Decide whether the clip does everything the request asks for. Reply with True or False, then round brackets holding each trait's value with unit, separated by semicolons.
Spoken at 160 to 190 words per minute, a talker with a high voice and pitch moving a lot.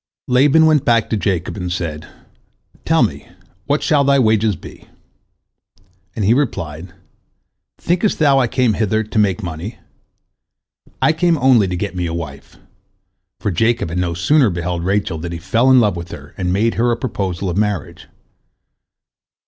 False (165 wpm; 105 Hz; 6.2 semitones)